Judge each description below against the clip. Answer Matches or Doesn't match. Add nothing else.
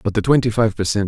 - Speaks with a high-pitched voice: Doesn't match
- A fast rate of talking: Matches